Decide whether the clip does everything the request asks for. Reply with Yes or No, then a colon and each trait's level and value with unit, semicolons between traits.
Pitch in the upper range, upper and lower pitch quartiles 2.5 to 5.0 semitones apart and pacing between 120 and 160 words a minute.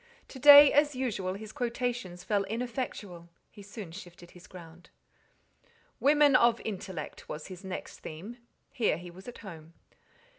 No: high, 200 Hz; wide, 5.6 semitones; average, 145 wpm